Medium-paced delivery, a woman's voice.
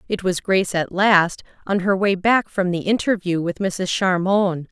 Yes: average, 190 wpm; female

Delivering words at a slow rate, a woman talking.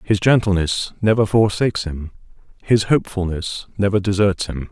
No: slow, 125 wpm; male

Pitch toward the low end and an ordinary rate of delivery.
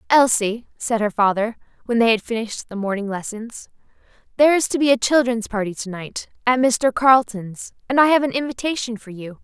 No: high, 230 Hz; average, 190 wpm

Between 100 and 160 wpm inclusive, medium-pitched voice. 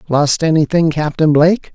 Yes: average, 140 wpm; medium, 155 Hz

